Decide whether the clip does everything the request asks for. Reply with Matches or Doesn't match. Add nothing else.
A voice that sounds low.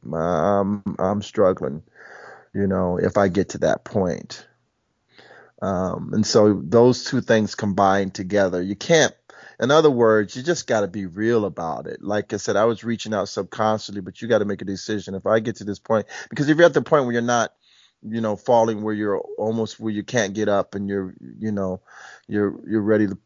Matches